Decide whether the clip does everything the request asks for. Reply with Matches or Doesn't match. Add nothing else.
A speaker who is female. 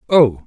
Doesn't match